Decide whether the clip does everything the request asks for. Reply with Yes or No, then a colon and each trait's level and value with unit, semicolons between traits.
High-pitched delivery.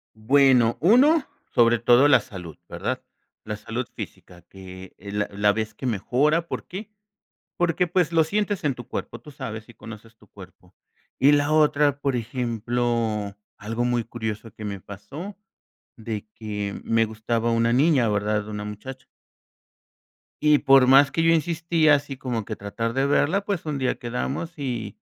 No: low, 120 Hz